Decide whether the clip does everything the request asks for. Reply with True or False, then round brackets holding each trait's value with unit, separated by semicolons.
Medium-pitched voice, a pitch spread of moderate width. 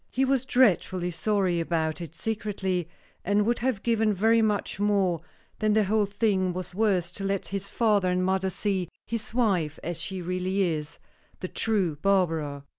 False (195 Hz; 3.3 semitones)